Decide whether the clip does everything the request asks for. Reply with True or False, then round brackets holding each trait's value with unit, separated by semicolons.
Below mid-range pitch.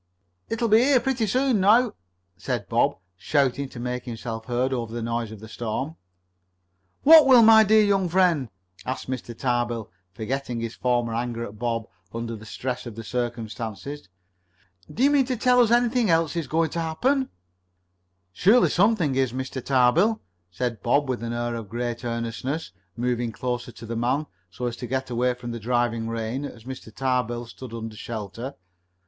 True (125 Hz)